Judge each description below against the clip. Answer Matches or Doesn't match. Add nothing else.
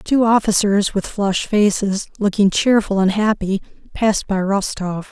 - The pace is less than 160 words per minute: Matches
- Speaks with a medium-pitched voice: Doesn't match